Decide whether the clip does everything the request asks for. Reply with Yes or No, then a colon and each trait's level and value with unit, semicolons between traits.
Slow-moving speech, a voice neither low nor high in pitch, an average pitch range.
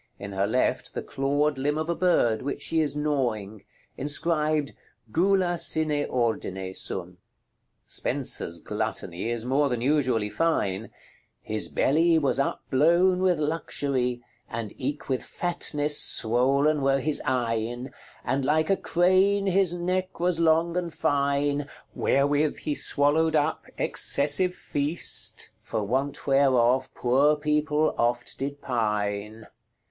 Yes: slow, 125 wpm; medium, 145 Hz; average, 4.5 semitones